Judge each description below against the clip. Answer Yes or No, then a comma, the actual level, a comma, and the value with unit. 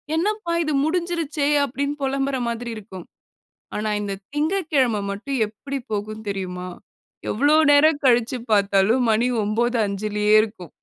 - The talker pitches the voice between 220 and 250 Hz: Yes, high, 240 Hz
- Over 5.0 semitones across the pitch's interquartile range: Yes, wide, 5.6 semitones